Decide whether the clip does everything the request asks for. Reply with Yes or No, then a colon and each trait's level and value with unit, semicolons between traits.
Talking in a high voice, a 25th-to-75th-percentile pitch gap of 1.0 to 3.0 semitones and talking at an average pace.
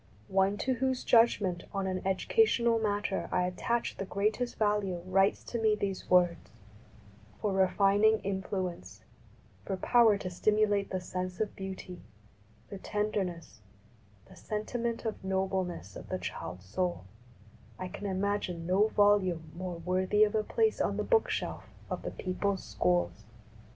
Yes: high, 195 Hz; average, 2.7 semitones; average, 150 wpm